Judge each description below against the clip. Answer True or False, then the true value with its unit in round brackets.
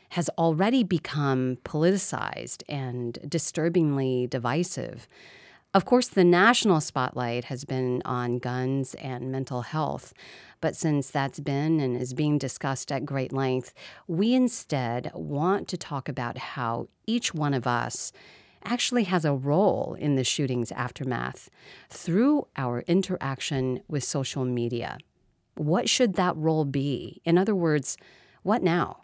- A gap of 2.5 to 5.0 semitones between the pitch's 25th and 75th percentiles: False (5.5 semitones)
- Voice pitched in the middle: True (145 Hz)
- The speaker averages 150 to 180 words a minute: False (135 wpm)